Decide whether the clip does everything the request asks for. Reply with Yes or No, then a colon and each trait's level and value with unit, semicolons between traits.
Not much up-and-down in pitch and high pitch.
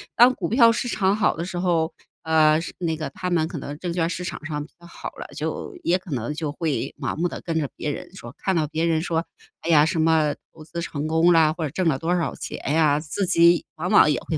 No: narrow, 2.2 semitones; medium, 165 Hz